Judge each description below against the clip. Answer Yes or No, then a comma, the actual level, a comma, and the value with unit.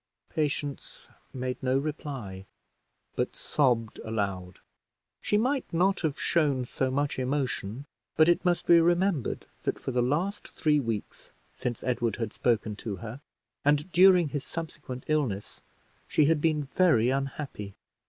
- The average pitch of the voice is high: No, medium, 140 Hz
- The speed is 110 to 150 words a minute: Yes, average, 140 wpm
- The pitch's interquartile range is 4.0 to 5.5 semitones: Yes, average, 5.1 semitones